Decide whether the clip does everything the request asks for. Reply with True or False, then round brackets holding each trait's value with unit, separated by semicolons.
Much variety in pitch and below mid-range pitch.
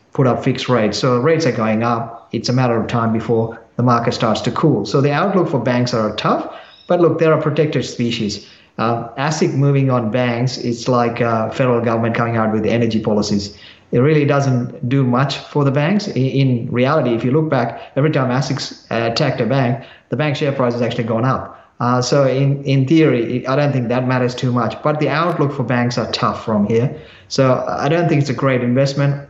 False (3.2 semitones; 125 Hz)